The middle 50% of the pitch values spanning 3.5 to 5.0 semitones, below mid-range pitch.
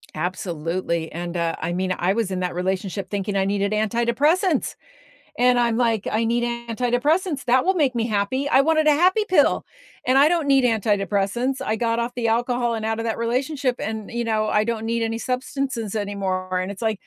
No: average, 4.2 semitones; high, 230 Hz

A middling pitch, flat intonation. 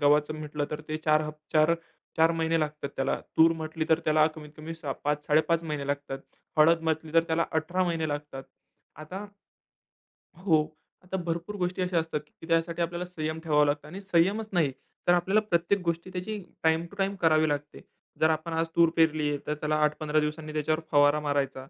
Yes: medium, 160 Hz; narrow, 1.9 semitones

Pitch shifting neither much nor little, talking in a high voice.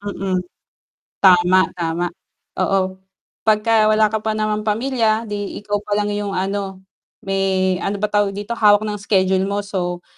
No: narrow, 1.9 semitones; high, 205 Hz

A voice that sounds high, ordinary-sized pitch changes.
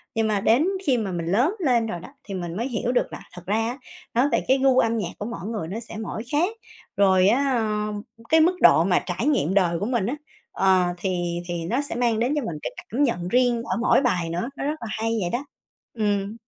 Yes: high, 220 Hz; average, 4.8 semitones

